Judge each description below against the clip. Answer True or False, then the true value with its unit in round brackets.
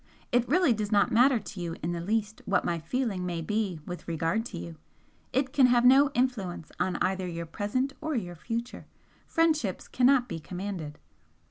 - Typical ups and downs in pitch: False (6.2 semitones)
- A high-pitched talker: True (205 Hz)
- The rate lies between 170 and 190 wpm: True (185 wpm)